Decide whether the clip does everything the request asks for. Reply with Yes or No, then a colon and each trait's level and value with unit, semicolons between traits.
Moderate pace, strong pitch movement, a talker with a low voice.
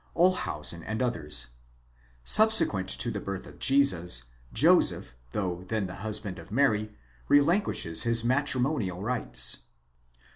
No: slow, 115 wpm; wide, 7.0 semitones; low, 105 Hz